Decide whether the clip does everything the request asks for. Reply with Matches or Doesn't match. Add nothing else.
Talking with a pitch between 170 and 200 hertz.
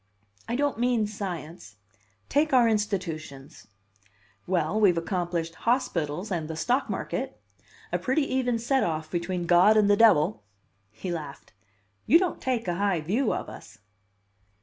Matches